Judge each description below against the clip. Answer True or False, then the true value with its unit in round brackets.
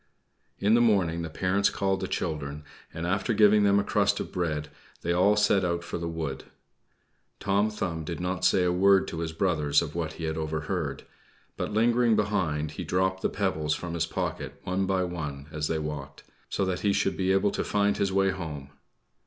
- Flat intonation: False (3.7 semitones)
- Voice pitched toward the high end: False (90 Hz)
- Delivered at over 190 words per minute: True (200 wpm)